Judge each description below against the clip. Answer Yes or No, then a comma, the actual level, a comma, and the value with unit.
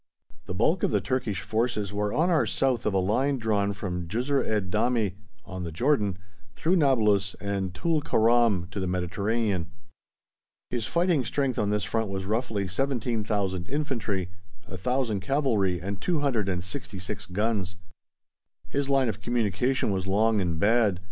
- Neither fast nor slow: Yes, average, 150 wpm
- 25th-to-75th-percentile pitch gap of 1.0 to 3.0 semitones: No, average, 4.7 semitones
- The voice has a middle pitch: No, low, 105 Hz